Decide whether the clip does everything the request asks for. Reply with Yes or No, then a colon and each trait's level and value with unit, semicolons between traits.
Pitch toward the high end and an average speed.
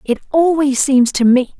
Yes: very high, 270 Hz; average, 190 wpm